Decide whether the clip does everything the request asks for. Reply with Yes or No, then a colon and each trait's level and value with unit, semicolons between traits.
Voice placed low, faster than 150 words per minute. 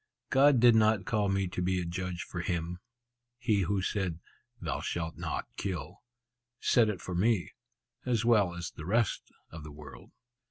Yes: very low, 95 Hz; average, 170 wpm